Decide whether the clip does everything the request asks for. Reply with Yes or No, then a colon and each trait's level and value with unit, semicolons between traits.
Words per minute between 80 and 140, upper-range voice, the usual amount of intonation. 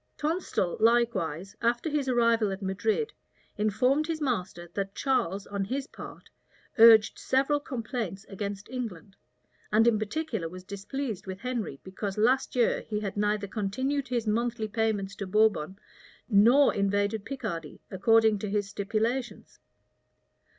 Yes: slow, 135 wpm; high, 215 Hz; average, 3.7 semitones